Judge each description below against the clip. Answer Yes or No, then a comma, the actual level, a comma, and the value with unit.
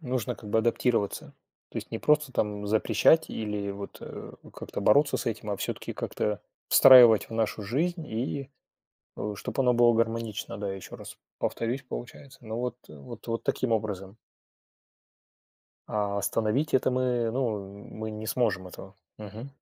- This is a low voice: Yes, low, 110 Hz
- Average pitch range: Yes, average, 3.4 semitones